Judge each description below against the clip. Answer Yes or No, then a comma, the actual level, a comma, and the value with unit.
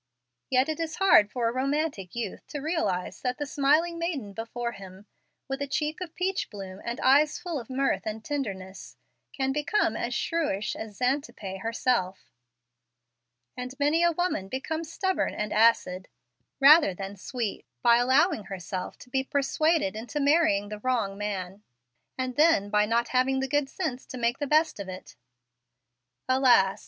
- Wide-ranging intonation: Yes, wide, 6.2 semitones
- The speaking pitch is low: No, very high, 255 Hz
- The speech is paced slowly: No, average, 165 wpm